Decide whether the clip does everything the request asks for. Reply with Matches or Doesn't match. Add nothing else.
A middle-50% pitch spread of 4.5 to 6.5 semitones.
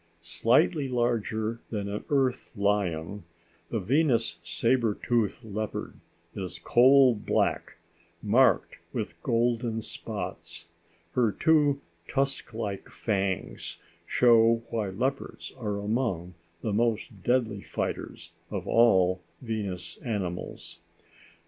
Doesn't match